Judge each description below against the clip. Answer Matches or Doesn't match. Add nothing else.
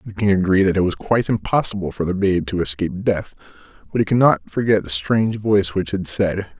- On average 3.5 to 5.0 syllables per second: Doesn't match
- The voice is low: Matches